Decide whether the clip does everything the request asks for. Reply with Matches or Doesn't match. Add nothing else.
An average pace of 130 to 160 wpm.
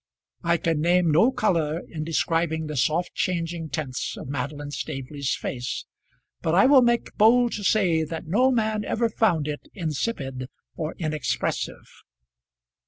Matches